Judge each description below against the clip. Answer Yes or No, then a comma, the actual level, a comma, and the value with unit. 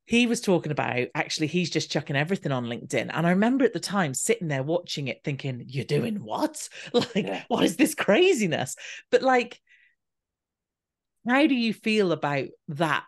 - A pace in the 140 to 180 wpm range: Yes, average, 175 wpm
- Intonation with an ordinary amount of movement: No, wide, 7.8 semitones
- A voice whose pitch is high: No, medium, 175 Hz